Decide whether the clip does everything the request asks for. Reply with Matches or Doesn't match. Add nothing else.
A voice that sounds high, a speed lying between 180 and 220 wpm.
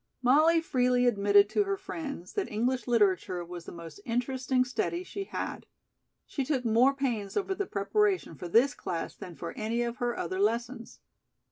Doesn't match